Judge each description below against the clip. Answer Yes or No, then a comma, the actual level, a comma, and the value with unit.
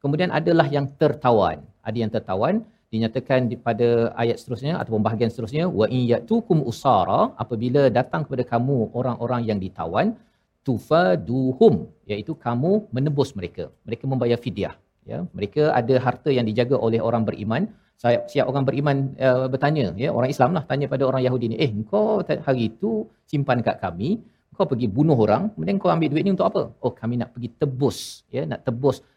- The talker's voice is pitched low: Yes, low, 130 Hz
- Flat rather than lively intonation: No, average, 4.3 semitones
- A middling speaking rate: No, fast, 165 wpm